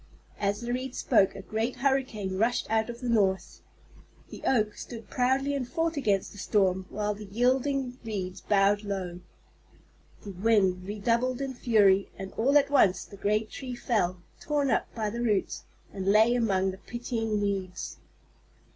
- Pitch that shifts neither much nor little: Yes, average, 3.9 semitones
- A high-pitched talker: Yes, high, 215 Hz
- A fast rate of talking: No, average, 165 wpm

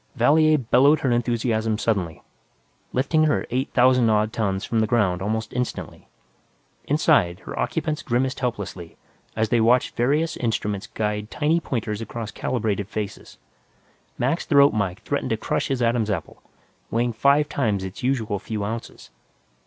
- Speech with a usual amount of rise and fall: Yes, average, 3.8 semitones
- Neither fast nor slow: Yes, average, 145 wpm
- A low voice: Yes, low, 115 Hz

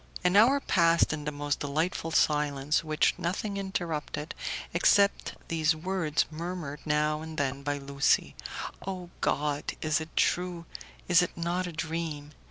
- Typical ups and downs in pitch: Yes, average, 3.0 semitones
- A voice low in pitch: No, medium, 160 Hz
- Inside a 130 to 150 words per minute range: Yes, average, 145 wpm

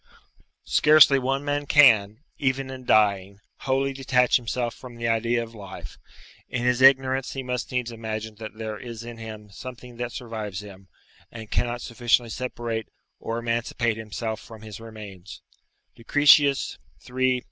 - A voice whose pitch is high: No, low, 120 Hz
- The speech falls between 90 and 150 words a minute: Yes, average, 145 wpm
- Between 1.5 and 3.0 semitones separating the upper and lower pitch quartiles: Yes, average, 2.7 semitones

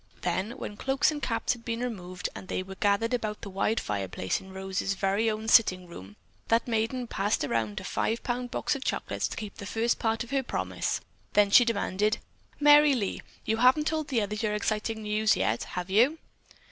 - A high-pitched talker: Yes, high, 215 Hz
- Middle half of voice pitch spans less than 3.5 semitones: No, average, 3.8 semitones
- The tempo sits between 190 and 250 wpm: Yes, average, 200 wpm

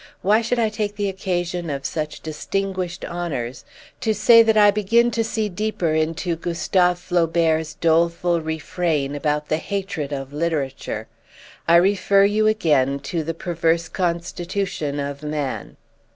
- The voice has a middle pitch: Yes, medium, 170 Hz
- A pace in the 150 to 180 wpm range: No, average, 140 wpm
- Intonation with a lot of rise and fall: No, average, 4.1 semitones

